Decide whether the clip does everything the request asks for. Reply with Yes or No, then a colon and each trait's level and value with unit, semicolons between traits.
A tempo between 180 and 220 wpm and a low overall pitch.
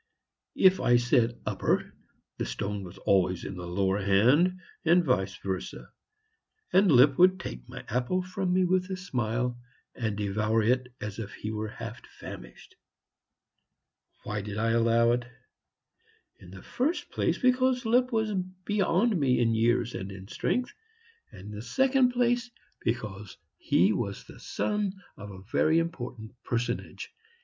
No: average, 150 wpm; low, 120 Hz